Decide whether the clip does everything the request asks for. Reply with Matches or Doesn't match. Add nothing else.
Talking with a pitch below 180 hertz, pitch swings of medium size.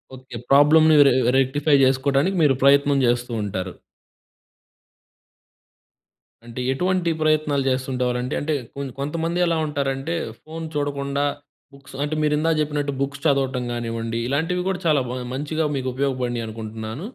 Matches